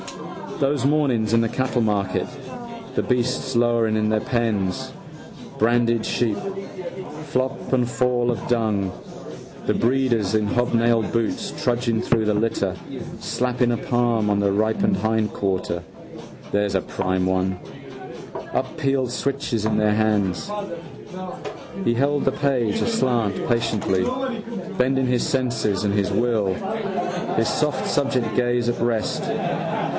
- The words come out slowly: Yes, slow, 120 wpm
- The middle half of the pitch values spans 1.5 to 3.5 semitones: Yes, average, 2.9 semitones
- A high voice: No, low, 115 Hz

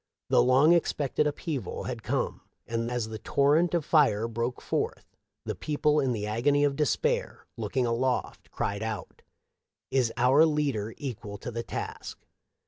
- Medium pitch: No, low, 130 Hz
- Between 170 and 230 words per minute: No, average, 155 wpm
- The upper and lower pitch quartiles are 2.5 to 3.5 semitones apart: No, average, 4.4 semitones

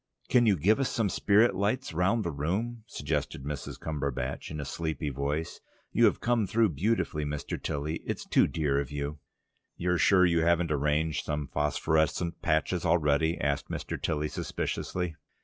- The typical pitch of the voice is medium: No, very low, 80 Hz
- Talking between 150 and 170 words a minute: Yes, average, 165 wpm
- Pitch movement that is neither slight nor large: Yes, average, 4.0 semitones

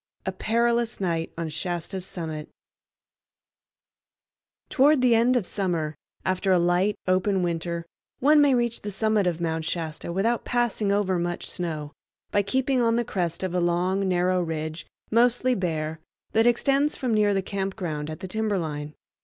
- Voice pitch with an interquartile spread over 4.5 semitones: Yes, average, 5.1 semitones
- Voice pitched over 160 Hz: Yes, high, 190 Hz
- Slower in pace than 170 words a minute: Yes, average, 160 wpm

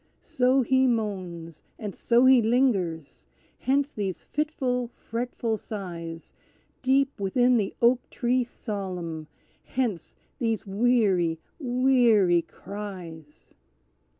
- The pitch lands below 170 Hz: No, high, 225 Hz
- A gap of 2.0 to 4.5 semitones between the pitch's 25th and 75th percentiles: No, wide, 5.5 semitones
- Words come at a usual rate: No, slow, 95 wpm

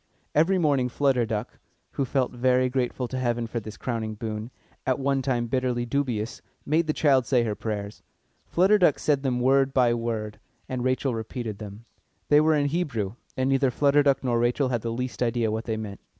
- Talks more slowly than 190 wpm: No, average, 195 wpm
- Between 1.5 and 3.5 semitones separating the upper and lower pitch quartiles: Yes, average, 3.0 semitones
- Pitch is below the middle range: Yes, low, 125 Hz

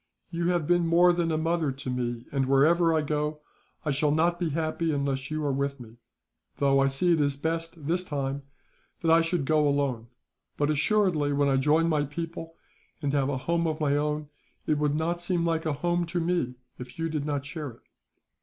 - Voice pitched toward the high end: No, medium, 150 Hz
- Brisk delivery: Yes, fast, 210 wpm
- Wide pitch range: No, average, 3.0 semitones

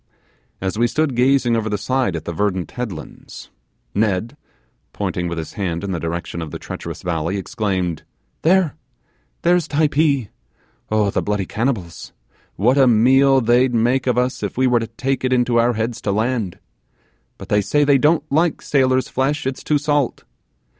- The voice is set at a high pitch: No, low, 120 Hz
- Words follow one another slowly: No, average, 175 wpm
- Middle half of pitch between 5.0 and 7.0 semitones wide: Yes, average, 5.3 semitones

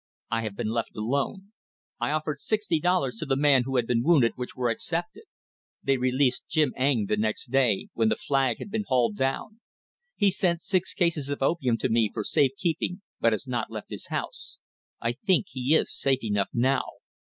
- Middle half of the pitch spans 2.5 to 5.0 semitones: No, wide, 5.5 semitones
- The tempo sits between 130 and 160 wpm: No, average, 200 wpm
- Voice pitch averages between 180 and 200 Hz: No, low, 135 Hz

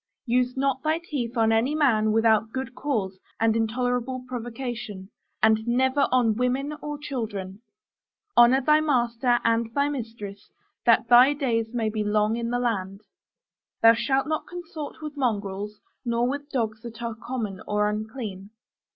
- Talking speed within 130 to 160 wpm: Yes, average, 150 wpm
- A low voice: No, high, 235 Hz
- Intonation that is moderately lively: Yes, average, 3.1 semitones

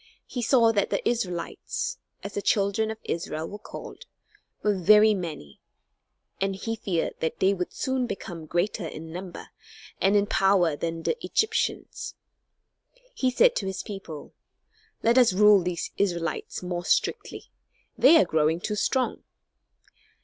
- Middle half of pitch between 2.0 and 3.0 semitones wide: No, average, 4.1 semitones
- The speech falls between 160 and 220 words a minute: No, average, 145 wpm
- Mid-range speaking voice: No, high, 195 Hz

